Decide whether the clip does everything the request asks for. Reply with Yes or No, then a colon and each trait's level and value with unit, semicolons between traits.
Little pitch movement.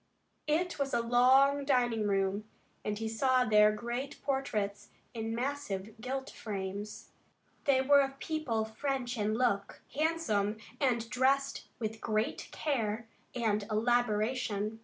No: average, 4.1 semitones